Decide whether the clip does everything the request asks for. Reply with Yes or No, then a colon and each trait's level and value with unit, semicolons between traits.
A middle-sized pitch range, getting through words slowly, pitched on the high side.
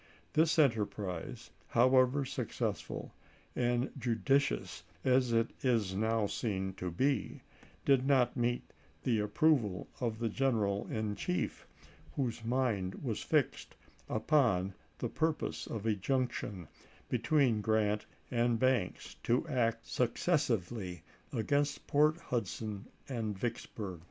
No: average, 3.9 semitones; slow, 115 wpm; low, 115 Hz